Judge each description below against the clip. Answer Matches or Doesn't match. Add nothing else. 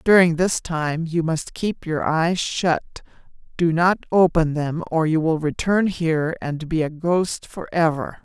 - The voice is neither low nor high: Matches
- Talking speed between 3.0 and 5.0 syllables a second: Matches